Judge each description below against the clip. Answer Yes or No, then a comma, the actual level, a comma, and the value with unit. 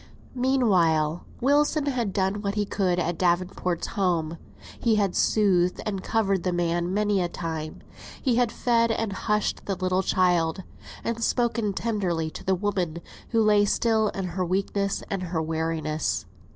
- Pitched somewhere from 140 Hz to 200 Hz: Yes, high, 190 Hz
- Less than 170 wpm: Yes, average, 155 wpm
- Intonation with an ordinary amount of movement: Yes, average, 3.5 semitones